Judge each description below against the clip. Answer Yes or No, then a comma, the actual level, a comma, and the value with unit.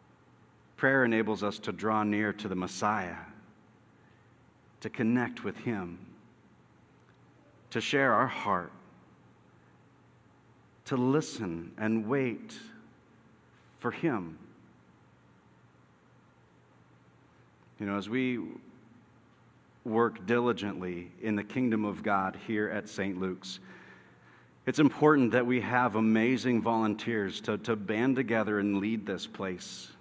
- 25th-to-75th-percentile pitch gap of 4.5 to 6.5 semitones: No, average, 3.5 semitones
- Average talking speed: No, slow, 105 wpm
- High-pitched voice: No, low, 110 Hz